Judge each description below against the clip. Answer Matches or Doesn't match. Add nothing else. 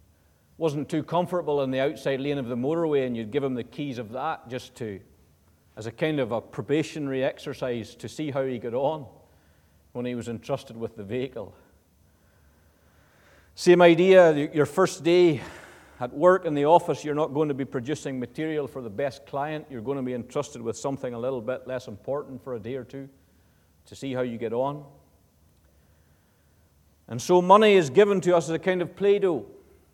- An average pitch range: Doesn't match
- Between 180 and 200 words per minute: Matches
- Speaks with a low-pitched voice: Matches